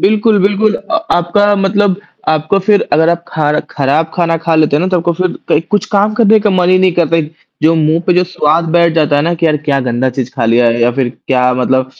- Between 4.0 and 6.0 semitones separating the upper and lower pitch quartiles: Yes, average, 4.3 semitones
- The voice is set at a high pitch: No, medium, 165 Hz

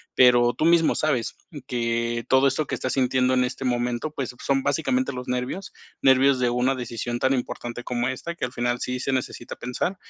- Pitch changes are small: Yes, narrow, 1.9 semitones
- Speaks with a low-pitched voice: Yes, low, 125 Hz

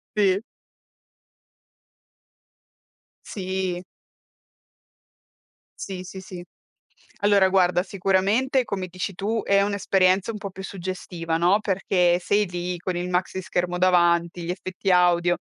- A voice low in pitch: No, medium, 185 Hz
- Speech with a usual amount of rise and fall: No, narrow, 1.8 semitones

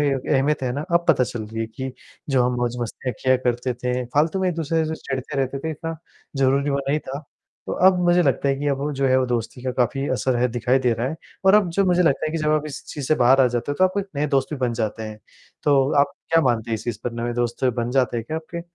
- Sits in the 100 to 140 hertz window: Yes, low, 135 Hz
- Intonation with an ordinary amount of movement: Yes, average, 3.8 semitones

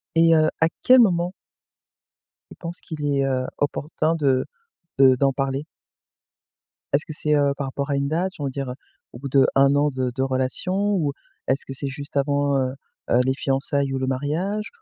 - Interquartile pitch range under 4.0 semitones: Yes, average, 2.7 semitones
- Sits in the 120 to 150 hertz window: Yes, medium, 140 Hz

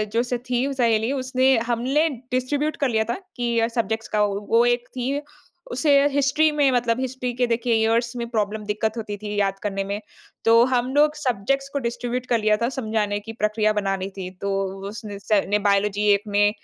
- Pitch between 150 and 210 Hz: No, high, 230 Hz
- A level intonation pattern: No, average, 3.4 semitones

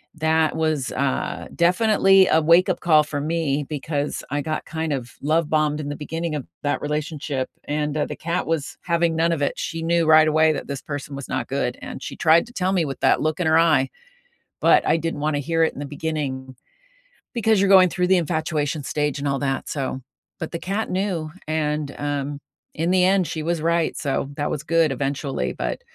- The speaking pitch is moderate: Yes, medium, 155 Hz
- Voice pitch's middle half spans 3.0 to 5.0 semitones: No, narrow, 2.6 semitones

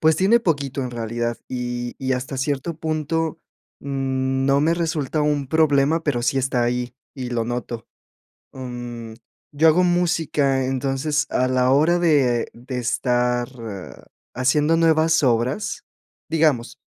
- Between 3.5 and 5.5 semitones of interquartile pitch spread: Yes, average, 4.1 semitones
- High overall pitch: No, low, 135 Hz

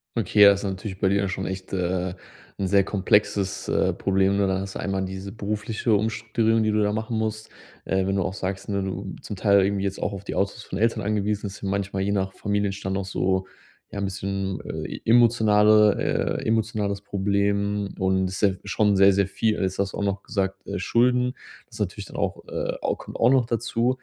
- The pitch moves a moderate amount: No, narrow, 1.8 semitones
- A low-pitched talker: Yes, low, 100 Hz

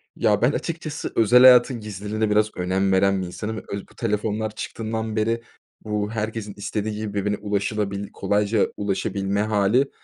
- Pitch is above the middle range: No, low, 105 Hz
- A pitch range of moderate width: No, narrow, 1.7 semitones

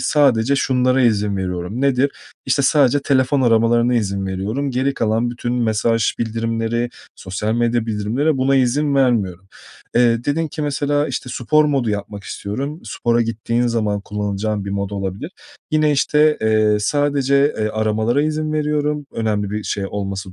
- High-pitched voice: No, low, 120 Hz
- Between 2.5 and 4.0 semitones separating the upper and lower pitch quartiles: No, average, 4.8 semitones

